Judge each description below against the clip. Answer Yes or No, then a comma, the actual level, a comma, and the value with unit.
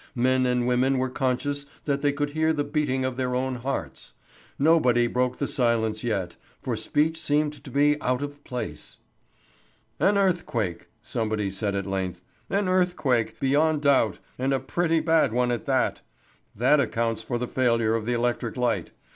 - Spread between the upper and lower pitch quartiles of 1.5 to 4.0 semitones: Yes, average, 3.6 semitones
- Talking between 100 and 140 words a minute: No, average, 170 wpm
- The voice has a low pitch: Yes, low, 130 Hz